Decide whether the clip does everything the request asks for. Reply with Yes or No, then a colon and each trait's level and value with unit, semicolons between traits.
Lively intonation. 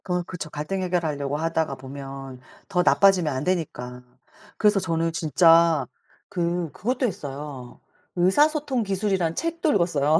No: average, 4.8 semitones